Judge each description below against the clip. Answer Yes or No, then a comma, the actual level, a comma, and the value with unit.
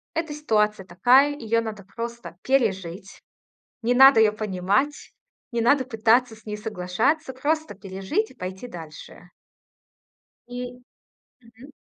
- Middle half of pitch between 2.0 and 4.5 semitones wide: No, average, 5.0 semitones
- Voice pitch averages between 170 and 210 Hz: No, high, 230 Hz